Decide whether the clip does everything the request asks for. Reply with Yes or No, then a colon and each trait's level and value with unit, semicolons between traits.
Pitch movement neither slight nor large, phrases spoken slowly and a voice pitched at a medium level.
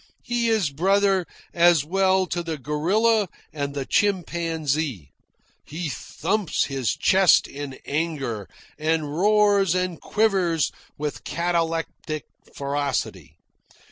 Yes: average, 4.6 semitones; slow, 105 wpm; medium, 165 Hz